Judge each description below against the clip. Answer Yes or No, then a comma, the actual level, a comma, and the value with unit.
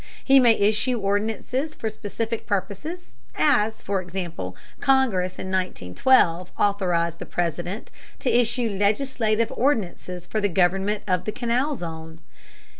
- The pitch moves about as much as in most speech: Yes, average, 4.7 semitones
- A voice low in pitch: No, high, 205 Hz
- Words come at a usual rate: No, slow, 125 wpm